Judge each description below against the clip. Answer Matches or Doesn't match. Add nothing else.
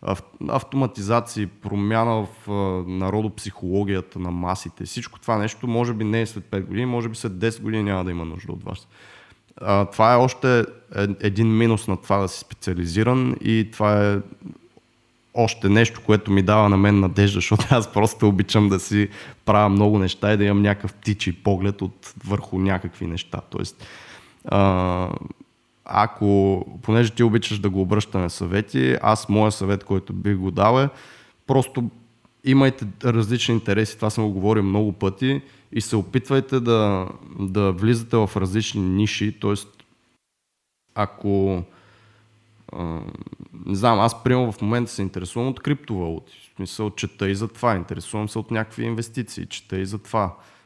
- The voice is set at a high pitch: Doesn't match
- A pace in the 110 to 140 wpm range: Doesn't match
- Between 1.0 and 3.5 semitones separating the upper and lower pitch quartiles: Matches